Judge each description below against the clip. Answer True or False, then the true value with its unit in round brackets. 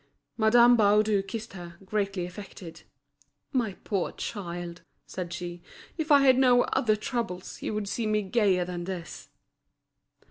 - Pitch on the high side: True (200 Hz)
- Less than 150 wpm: True (140 wpm)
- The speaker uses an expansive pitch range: False (4.3 semitones)